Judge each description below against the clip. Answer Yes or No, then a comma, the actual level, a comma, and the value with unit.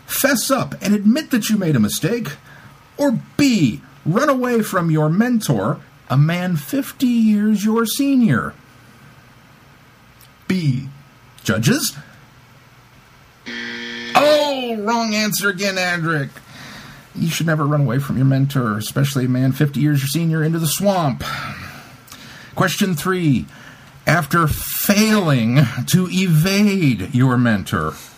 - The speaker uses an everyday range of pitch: No, wide, 7.8 semitones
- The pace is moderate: No, slow, 115 wpm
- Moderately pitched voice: Yes, medium, 160 Hz